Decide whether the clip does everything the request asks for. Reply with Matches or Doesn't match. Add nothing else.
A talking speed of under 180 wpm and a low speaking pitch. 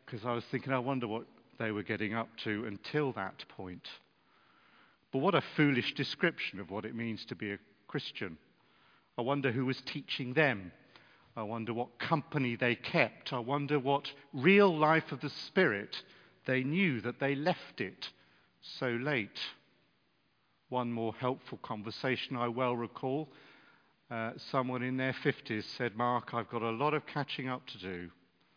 Matches